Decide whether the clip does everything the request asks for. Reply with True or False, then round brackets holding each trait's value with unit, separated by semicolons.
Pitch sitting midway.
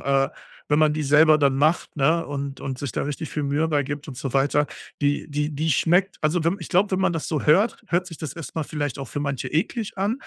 True (150 Hz)